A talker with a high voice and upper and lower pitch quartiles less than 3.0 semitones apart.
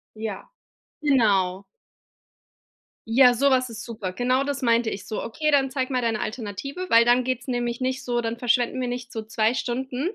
Yes: high, 245 Hz; narrow, 2.4 semitones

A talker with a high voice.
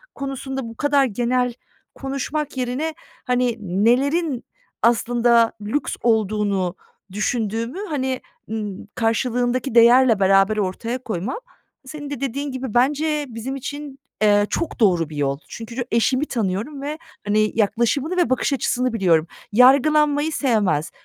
Yes: high, 245 Hz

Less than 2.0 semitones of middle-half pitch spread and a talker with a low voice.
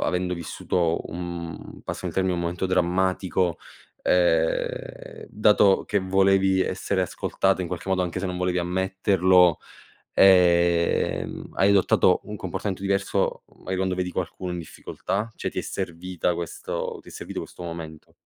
Yes: narrow, 1.5 semitones; very low, 90 Hz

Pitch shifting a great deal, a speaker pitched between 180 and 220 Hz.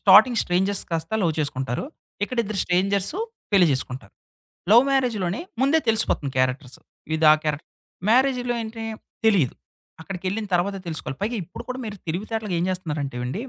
Yes: wide, 6.0 semitones; high, 190 Hz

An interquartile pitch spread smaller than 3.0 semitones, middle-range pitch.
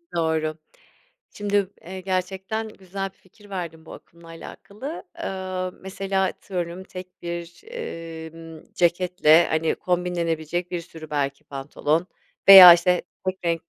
Yes: narrow, 2.5 semitones; medium, 175 Hz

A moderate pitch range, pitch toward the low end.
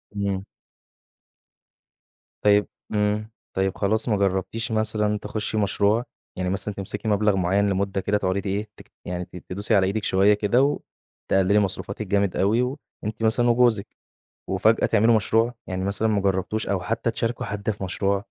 No: narrow, 2.1 semitones; low, 100 Hz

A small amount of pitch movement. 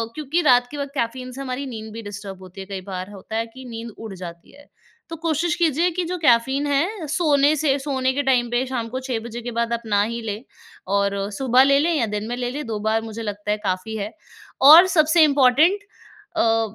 No: average, 4.7 semitones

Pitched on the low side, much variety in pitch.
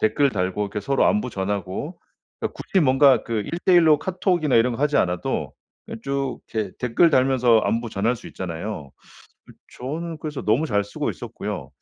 Yes: low, 125 Hz; wide, 6.3 semitones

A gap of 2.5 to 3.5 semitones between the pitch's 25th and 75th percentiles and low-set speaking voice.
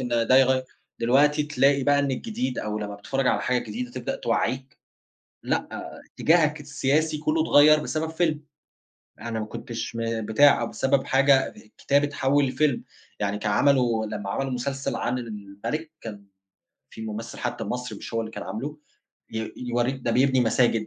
No: average, 4.0 semitones; low, 130 Hz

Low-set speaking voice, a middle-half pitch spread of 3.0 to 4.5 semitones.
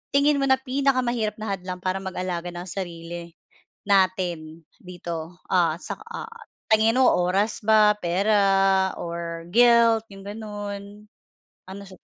No: high, 195 Hz; average, 3.8 semitones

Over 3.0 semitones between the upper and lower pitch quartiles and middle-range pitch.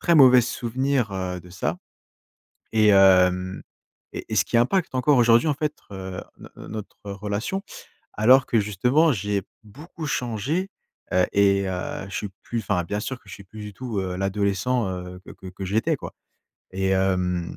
No: average, 4.8 semitones; low, 105 Hz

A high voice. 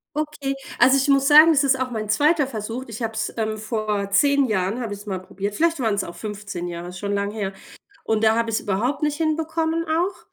Yes: high, 225 Hz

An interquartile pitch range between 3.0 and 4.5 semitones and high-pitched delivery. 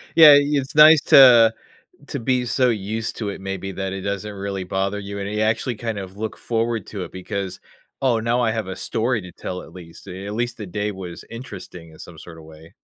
No: average, 3.5 semitones; low, 105 Hz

